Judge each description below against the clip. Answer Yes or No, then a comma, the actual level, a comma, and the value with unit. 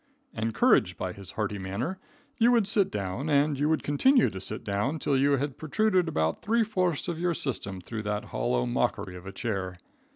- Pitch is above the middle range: No, low, 125 Hz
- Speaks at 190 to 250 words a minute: Yes, average, 195 wpm